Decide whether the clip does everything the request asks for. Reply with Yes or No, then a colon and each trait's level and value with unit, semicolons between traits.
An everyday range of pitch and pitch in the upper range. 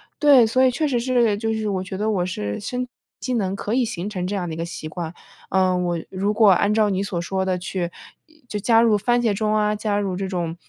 Yes: average, 3.5 semitones; high, 205 Hz